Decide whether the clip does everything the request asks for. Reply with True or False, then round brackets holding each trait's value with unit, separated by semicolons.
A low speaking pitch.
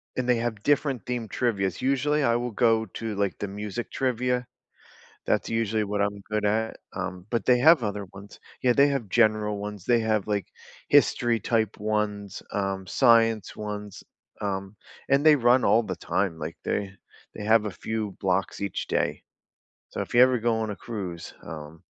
True (110 Hz)